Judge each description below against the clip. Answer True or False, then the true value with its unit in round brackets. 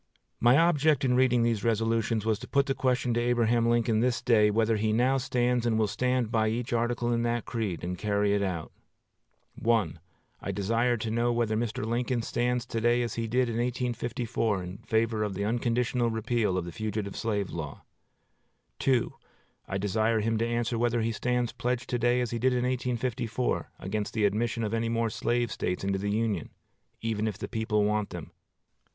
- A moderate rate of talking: True (190 wpm)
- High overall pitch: False (115 Hz)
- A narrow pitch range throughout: True (2.1 semitones)